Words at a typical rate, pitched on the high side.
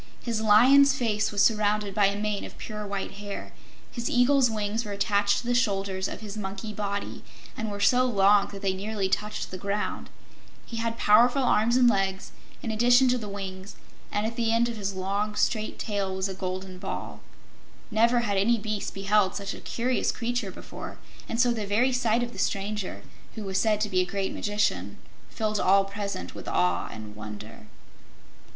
Yes: average, 190 wpm; high, 210 Hz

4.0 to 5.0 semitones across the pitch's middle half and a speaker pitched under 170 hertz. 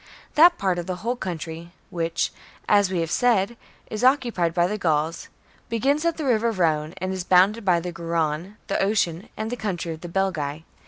No: average, 4.6 semitones; medium, 185 Hz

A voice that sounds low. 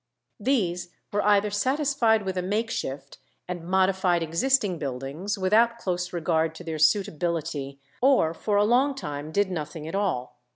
No: medium, 185 Hz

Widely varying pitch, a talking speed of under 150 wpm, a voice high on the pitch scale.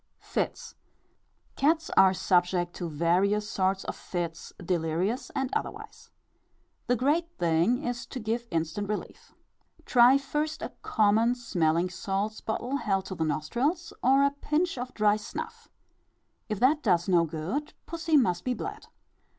Yes: wide, 7.0 semitones; average, 140 wpm; high, 210 Hz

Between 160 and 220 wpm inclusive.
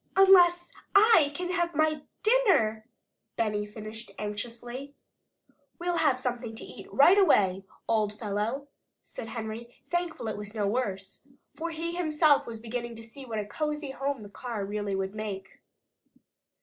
No: average, 150 wpm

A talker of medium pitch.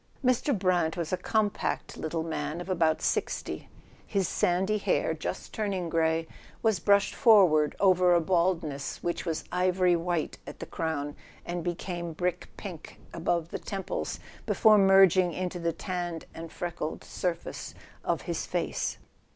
Yes: medium, 175 Hz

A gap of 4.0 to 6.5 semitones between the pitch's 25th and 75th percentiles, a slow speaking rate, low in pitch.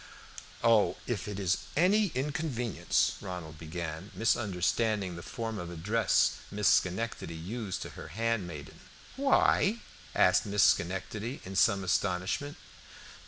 Yes: average, 4.5 semitones; slow, 120 wpm; low, 100 Hz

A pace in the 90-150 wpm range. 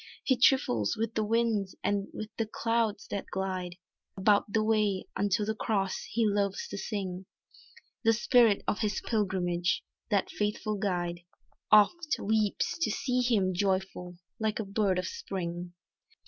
Yes: average, 145 wpm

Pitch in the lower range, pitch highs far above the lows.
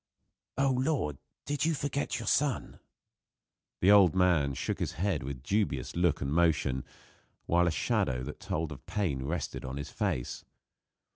Yes: very low, 85 Hz; wide, 6.8 semitones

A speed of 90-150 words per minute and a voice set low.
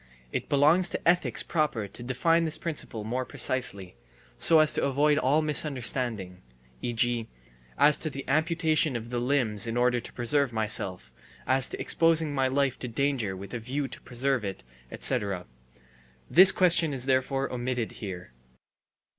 No: average, 160 wpm; low, 130 Hz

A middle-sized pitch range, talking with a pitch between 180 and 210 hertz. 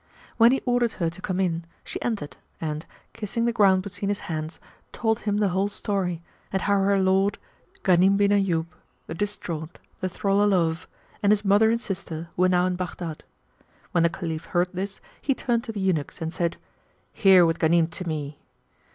Yes: average, 3.3 semitones; high, 190 Hz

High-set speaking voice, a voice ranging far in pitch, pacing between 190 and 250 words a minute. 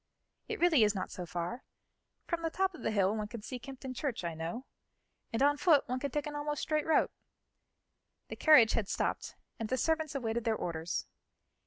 Yes: very high, 255 Hz; wide, 5.9 semitones; average, 200 wpm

